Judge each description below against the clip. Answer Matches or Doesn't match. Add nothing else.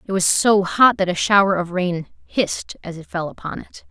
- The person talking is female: Matches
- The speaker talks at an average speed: Doesn't match